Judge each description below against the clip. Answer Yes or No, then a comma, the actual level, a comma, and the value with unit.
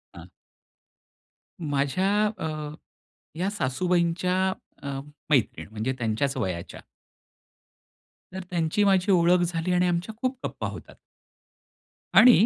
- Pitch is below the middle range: No, medium, 170 Hz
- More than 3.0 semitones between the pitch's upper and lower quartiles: Yes, average, 5.1 semitones